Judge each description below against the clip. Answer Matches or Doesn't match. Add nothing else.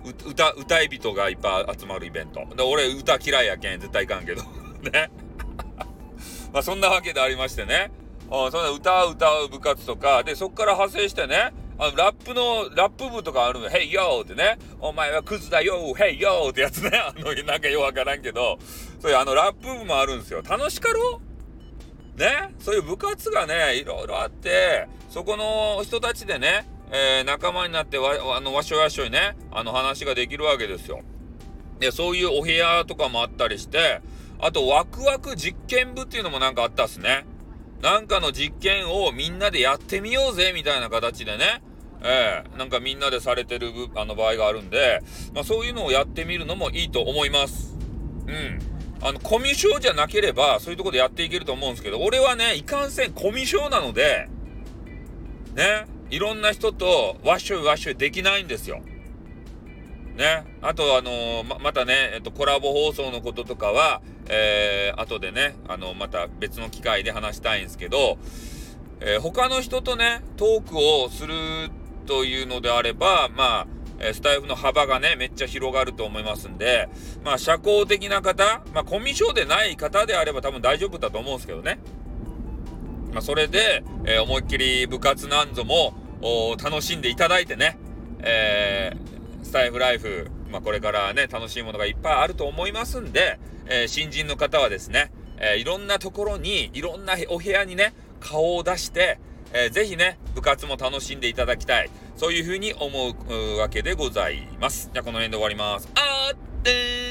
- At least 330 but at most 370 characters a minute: Matches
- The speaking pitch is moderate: Matches